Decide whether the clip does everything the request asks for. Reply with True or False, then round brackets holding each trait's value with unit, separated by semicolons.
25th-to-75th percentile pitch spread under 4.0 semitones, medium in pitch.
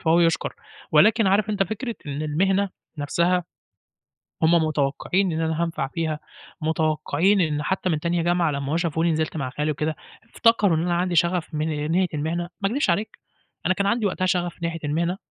True (3.1 semitones; 170 Hz)